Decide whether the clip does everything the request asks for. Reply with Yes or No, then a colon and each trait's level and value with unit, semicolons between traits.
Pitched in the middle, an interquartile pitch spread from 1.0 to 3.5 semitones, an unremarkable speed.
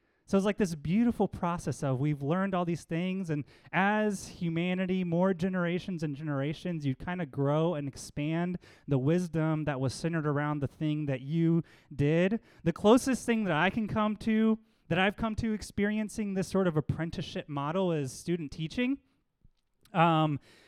No: medium, 170 Hz; average, 4.3 semitones; average, 170 wpm